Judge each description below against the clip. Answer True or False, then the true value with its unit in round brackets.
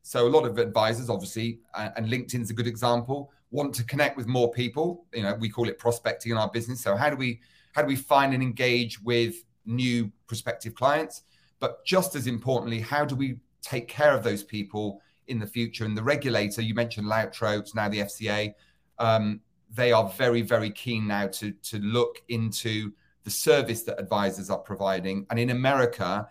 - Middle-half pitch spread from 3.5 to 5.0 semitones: False (2.6 semitones)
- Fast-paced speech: False (190 wpm)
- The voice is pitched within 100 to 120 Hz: True (115 Hz)